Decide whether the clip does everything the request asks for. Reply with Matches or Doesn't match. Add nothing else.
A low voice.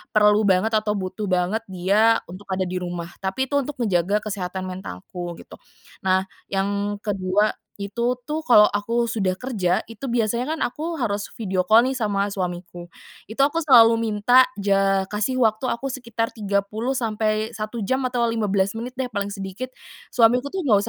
Doesn't match